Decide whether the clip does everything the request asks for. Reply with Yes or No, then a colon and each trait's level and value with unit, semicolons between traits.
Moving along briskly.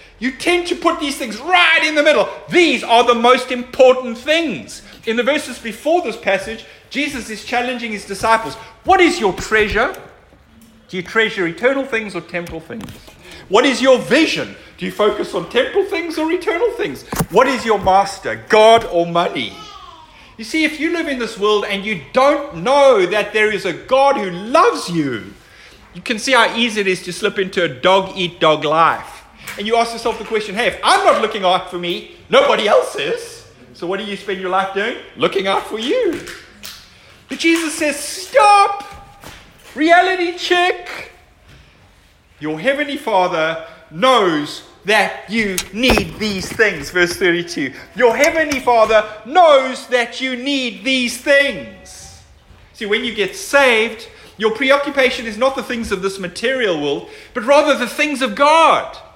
No: average, 170 wpm